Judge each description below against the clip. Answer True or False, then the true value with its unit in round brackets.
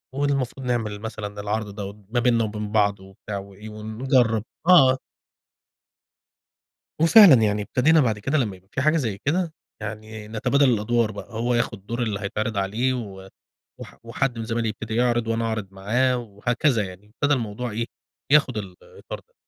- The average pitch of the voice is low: True (115 Hz)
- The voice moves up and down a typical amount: True (3.3 semitones)